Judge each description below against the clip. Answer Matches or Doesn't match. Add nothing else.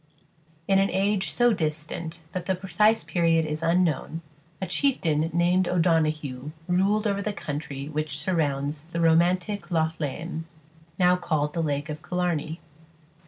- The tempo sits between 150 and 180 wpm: Doesn't match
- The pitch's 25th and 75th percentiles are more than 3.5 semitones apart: Doesn't match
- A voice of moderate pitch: Matches